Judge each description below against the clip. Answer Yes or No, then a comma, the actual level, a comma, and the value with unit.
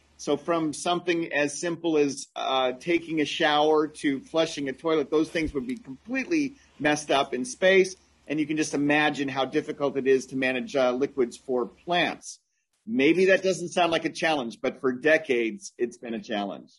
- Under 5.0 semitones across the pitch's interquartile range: Yes, average, 4.2 semitones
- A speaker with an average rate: Yes, average, 185 wpm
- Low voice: No, medium, 155 Hz